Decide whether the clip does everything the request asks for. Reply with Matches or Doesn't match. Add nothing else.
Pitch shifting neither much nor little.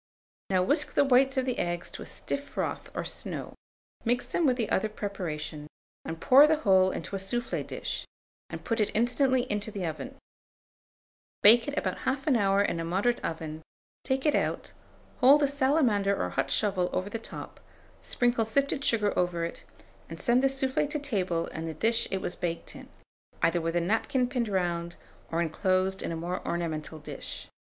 Doesn't match